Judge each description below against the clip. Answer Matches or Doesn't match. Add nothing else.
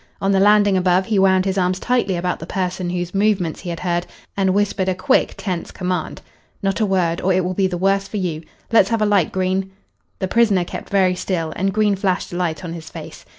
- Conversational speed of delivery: Doesn't match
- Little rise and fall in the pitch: Matches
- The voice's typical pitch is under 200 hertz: Matches